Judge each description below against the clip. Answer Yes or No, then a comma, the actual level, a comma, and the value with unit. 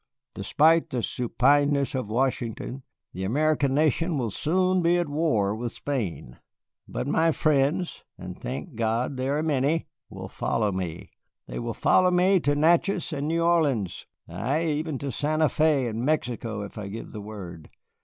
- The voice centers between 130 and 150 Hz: Yes, medium, 140 Hz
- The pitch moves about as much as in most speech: No, wide, 5.7 semitones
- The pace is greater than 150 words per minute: Yes, average, 160 wpm